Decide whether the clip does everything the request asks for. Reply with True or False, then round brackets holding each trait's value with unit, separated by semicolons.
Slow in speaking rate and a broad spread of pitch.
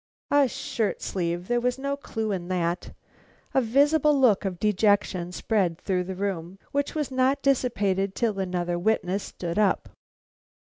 False (150 wpm; 5.9 semitones)